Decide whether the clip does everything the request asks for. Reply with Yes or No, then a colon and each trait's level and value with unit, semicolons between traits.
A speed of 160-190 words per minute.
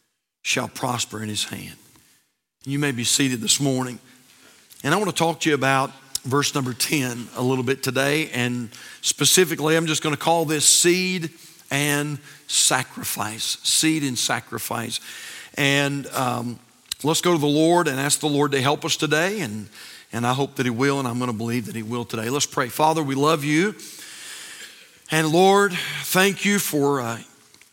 Yes: average, 180 wpm